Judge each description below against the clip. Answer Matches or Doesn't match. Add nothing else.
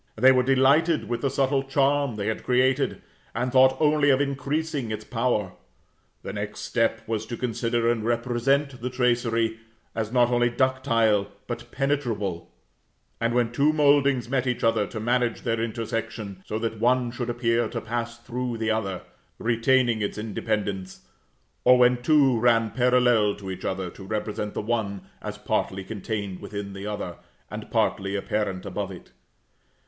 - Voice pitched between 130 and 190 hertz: Doesn't match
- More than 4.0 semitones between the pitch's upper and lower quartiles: Doesn't match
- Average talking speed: Matches